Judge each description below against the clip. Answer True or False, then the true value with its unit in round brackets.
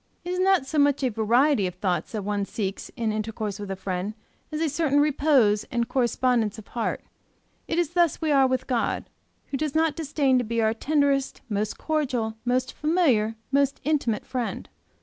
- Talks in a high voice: True (255 Hz)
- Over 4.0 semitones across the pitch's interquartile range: True (5.2 semitones)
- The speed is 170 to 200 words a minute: True (190 wpm)